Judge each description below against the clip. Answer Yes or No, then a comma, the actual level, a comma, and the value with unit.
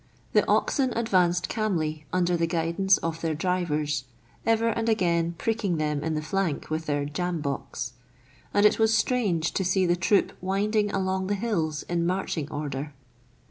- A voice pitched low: No, medium, 175 Hz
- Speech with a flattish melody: No, average, 4.2 semitones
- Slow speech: No, average, 170 wpm